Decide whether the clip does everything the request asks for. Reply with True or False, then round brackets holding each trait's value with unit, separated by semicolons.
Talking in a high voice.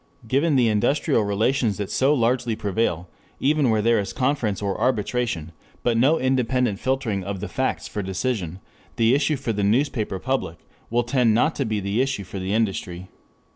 False (115 Hz)